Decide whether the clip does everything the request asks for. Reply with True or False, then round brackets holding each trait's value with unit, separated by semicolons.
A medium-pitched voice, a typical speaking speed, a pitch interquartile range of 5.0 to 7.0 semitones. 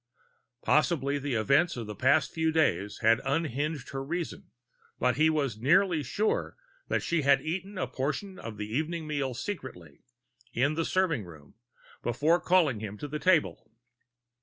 True (145 Hz; 160 wpm; 5.3 semitones)